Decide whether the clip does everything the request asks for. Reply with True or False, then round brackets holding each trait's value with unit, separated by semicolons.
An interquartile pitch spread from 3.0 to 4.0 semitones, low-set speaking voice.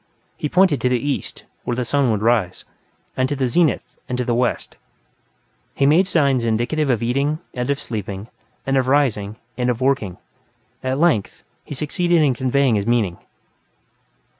True (3.5 semitones; 130 Hz)